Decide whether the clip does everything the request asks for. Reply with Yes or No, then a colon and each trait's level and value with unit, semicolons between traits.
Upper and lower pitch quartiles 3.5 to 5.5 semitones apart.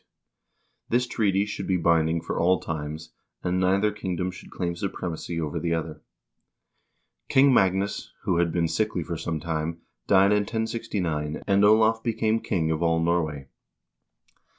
Yes: average, 4.0 semitones